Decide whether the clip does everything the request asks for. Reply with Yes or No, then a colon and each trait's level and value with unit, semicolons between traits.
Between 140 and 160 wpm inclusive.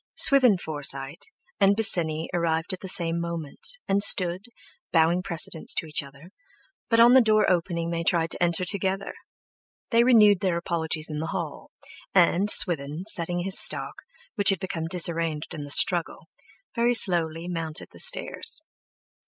Yes: average, 145 wpm